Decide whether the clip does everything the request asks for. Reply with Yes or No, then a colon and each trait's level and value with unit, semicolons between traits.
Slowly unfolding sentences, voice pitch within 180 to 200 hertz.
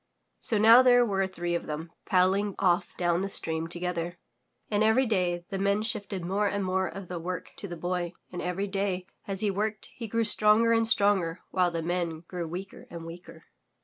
No: fast, 205 wpm; medium, 185 Hz